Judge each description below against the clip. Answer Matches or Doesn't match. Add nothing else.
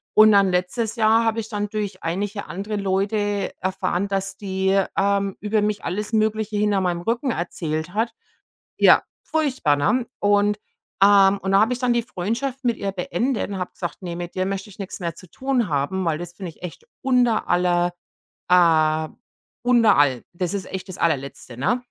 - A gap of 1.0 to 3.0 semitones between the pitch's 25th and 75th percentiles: Doesn't match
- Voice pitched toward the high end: Matches